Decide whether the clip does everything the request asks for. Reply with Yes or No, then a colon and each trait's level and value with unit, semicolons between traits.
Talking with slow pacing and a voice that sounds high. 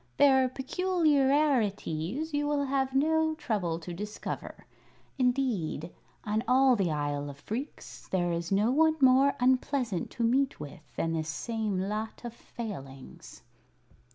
Yes: slow, 130 wpm; high, 235 Hz